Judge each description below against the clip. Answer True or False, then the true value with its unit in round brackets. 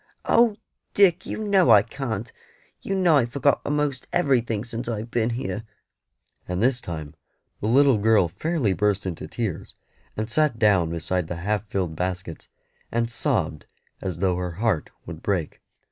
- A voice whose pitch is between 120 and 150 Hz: False (110 Hz)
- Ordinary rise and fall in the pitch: False (6.4 semitones)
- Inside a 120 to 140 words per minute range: False (160 wpm)